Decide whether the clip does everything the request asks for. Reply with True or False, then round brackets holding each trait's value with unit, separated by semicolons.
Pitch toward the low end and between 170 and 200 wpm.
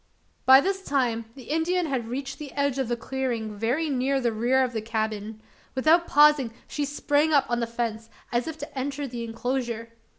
False (260 Hz; 195 wpm)